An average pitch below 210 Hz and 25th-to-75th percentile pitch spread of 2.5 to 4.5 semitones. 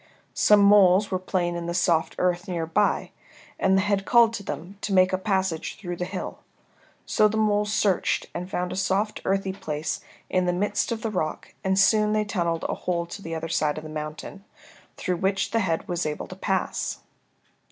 Yes: high, 190 Hz; average, 2.9 semitones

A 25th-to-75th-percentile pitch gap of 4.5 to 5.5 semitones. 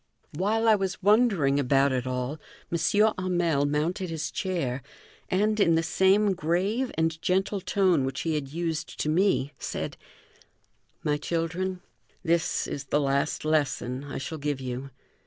Yes: average, 4.9 semitones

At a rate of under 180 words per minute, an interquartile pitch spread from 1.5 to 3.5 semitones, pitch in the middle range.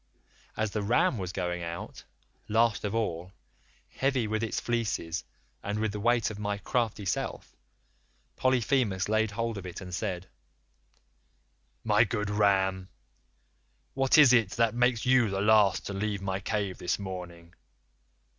No: average, 145 wpm; average, 3.2 semitones; low, 105 Hz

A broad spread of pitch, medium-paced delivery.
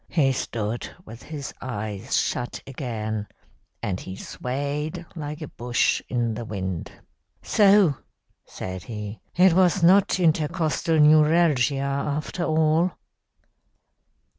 No: wide, 5.9 semitones; slow, 110 wpm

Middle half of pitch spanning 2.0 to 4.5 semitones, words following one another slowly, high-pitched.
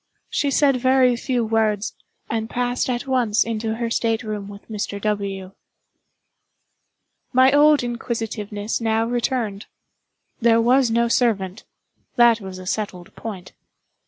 Yes: average, 2.7 semitones; slow, 125 wpm; high, 225 Hz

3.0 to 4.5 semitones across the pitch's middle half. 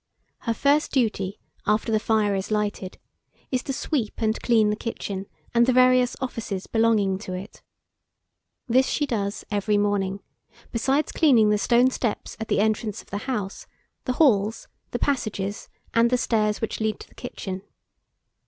Yes: average, 3.3 semitones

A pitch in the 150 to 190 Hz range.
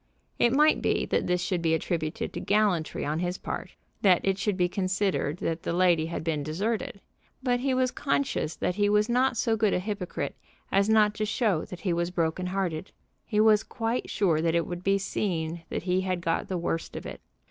Yes: medium, 185 Hz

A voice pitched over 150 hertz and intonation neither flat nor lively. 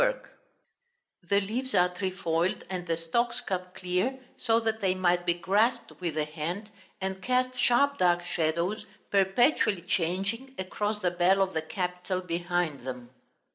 Yes: medium, 185 Hz; average, 3.9 semitones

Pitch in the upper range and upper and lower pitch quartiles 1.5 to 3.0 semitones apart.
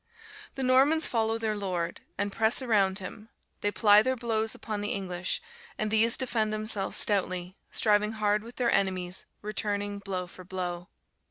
Yes: high, 210 Hz; average, 2.7 semitones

